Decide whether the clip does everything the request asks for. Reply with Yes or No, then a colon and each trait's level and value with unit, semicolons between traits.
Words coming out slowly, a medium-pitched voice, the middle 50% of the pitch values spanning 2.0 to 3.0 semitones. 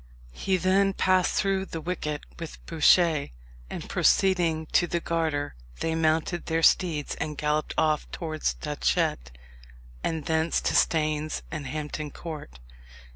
Yes: slow, 130 wpm; medium, 160 Hz; narrow, 2.4 semitones